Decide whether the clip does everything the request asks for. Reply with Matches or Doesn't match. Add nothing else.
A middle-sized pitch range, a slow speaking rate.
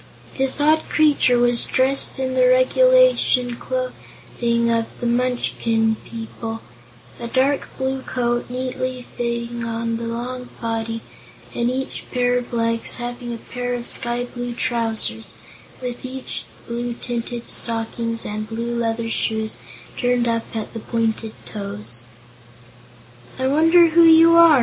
Doesn't match